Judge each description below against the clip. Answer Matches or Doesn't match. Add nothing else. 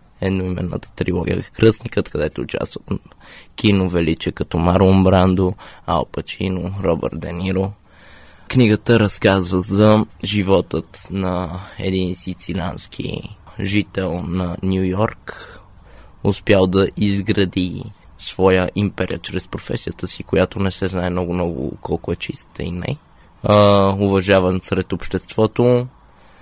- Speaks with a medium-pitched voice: Doesn't match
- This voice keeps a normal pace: Doesn't match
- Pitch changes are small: Matches